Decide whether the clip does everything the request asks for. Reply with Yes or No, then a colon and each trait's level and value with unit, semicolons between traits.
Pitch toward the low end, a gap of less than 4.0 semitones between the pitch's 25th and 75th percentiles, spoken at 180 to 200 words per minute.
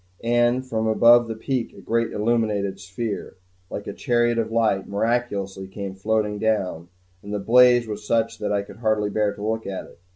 Yes: low, 110 Hz; narrow, 2.4 semitones; average, 190 wpm